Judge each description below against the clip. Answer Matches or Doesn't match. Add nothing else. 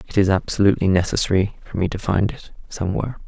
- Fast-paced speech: Doesn't match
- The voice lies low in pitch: Matches